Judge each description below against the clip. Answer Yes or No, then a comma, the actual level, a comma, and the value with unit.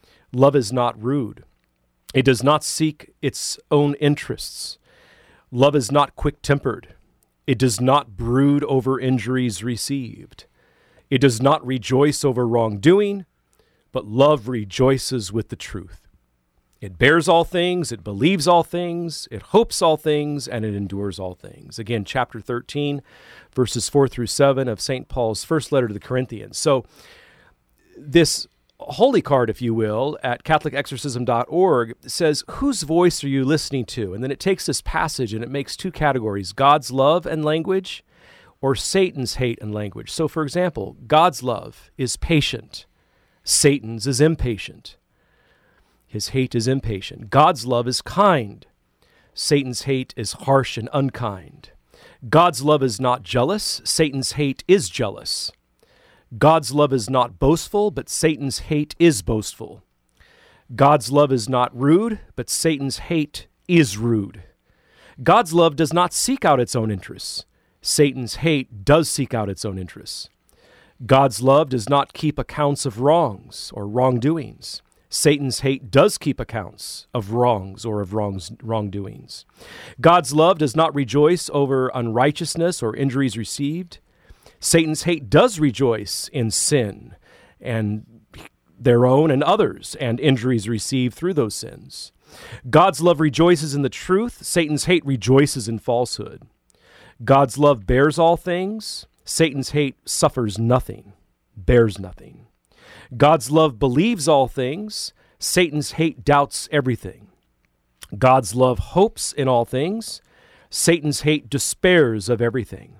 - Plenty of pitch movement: No, average, 4.6 semitones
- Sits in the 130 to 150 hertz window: Yes, low, 135 Hz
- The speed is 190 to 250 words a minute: No, average, 140 wpm